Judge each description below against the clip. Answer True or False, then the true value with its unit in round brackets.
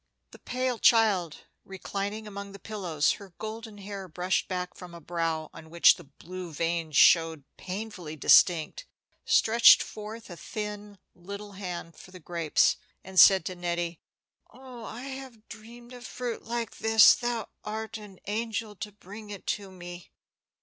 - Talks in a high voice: True (200 Hz)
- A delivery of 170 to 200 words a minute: False (155 wpm)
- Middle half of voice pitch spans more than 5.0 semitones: False (4.1 semitones)